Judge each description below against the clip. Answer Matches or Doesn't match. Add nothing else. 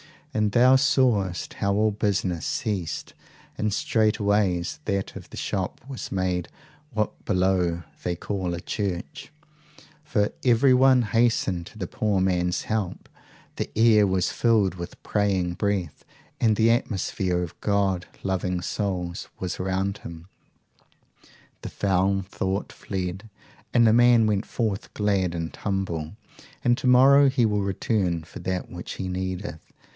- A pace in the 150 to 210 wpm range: Doesn't match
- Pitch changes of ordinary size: Matches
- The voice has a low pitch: Matches